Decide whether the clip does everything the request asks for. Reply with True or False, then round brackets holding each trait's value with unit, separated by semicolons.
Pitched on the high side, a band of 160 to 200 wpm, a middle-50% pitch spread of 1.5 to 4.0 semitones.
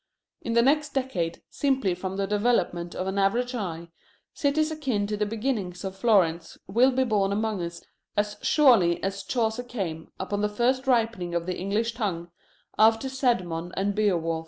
False (205 Hz; 170 wpm; 4.9 semitones)